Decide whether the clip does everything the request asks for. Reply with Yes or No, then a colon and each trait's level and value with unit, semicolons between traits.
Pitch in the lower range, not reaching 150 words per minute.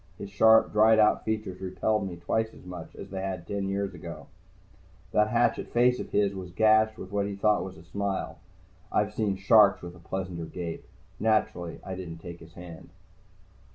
No: very low, 95 Hz; average, 190 wpm